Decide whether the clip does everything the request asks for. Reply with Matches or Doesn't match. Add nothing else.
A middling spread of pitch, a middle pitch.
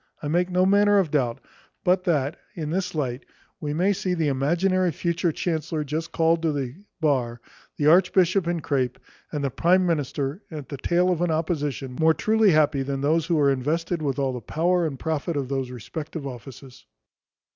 Matches